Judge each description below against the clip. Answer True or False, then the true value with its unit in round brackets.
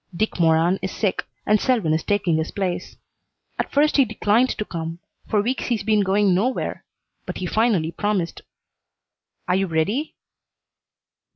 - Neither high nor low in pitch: False (200 Hz)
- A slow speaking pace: False (155 wpm)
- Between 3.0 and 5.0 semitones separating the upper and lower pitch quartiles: True (4.3 semitones)